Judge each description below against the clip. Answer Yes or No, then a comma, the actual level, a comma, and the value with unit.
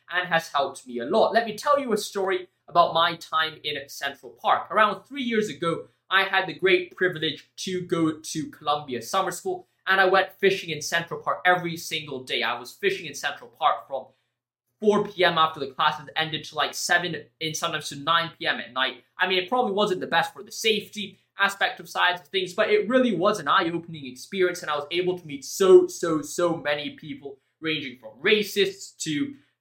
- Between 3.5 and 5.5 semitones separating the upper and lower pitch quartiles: Yes, average, 4.1 semitones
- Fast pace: Yes, fast, 210 wpm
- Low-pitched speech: No, medium, 175 Hz